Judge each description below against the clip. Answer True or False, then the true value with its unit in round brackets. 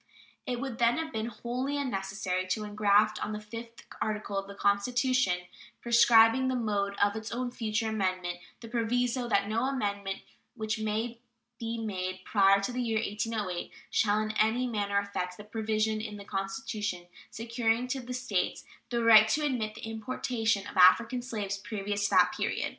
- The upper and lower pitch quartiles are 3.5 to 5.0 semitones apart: False (2.8 semitones)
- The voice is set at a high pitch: True (220 Hz)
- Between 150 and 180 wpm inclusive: True (170 wpm)